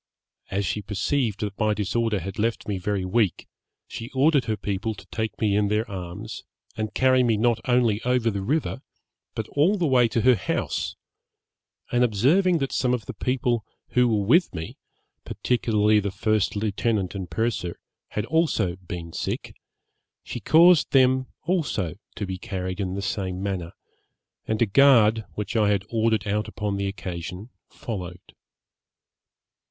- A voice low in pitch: Yes, low, 110 Hz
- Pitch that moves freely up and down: No, average, 3.8 semitones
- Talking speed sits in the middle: Yes, average, 160 wpm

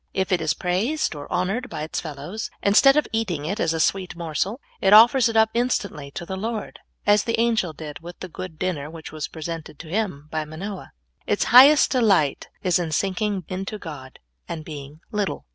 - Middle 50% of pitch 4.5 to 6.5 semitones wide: Yes, wide, 5.4 semitones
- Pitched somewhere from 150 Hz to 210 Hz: Yes, medium, 185 Hz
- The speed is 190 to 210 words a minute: Yes, average, 195 wpm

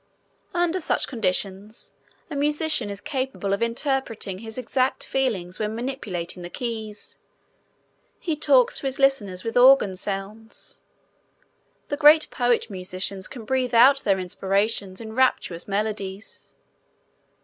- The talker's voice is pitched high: Yes, high, 225 Hz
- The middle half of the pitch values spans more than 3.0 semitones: Yes, average, 5.3 semitones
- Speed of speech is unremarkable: No, slow, 125 wpm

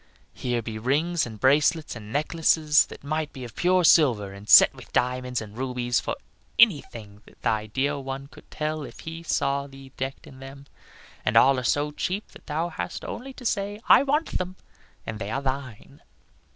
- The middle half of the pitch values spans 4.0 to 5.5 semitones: Yes, average, 4.5 semitones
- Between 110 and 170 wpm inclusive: No, average, 190 wpm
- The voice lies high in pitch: No, low, 135 Hz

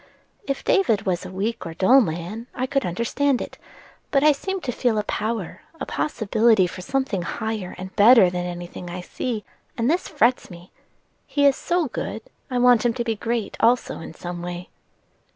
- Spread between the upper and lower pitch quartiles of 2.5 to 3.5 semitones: No, wide, 5.6 semitones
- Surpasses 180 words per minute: Yes, average, 190 wpm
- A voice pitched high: Yes, high, 225 Hz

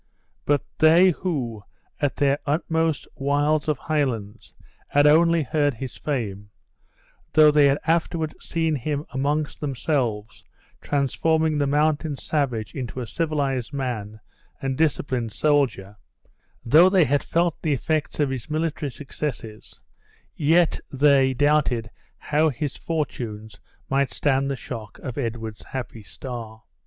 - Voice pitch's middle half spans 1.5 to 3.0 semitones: No, average, 4.0 semitones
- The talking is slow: Yes, slow, 125 wpm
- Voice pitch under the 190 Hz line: Yes, medium, 140 Hz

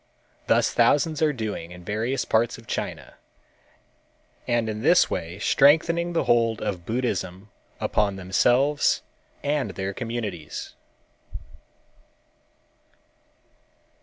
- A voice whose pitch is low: Yes, low, 115 Hz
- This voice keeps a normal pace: No, slow, 100 wpm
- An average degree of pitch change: No, wide, 5.7 semitones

